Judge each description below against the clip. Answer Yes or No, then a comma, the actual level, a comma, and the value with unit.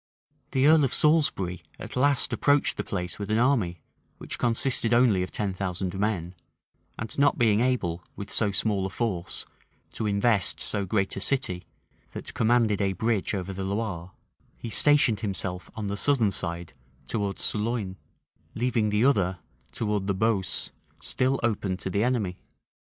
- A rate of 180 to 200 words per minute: No, average, 160 wpm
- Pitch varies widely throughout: No, average, 3.9 semitones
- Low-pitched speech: Yes, low, 105 Hz